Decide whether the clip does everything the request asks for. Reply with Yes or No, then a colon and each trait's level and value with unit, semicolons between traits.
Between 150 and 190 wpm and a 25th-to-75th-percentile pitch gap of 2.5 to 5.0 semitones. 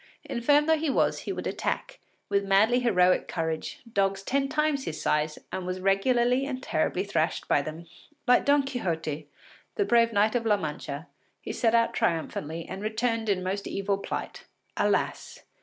No: average, 170 wpm; wide, 5.6 semitones